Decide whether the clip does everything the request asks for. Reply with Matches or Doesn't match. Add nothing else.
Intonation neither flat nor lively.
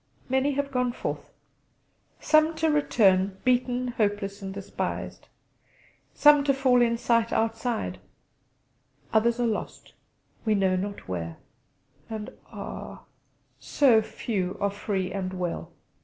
Matches